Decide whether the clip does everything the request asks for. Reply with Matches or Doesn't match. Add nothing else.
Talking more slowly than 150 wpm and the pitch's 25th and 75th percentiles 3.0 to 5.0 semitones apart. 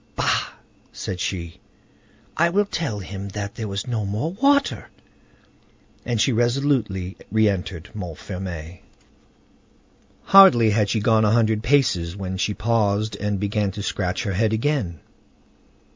Matches